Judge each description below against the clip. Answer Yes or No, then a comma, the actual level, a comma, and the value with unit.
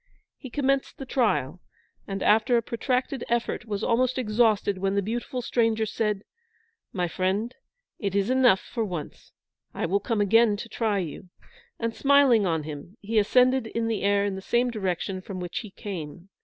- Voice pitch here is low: No, high, 215 Hz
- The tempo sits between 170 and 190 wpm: Yes, average, 175 wpm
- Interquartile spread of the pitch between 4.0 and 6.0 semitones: No, average, 3.6 semitones